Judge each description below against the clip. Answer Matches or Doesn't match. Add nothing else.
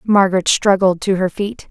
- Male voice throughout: Doesn't match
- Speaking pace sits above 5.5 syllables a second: Doesn't match